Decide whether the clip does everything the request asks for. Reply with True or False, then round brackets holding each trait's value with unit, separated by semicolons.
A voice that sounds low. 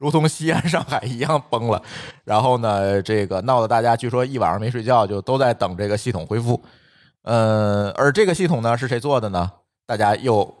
True (120 Hz)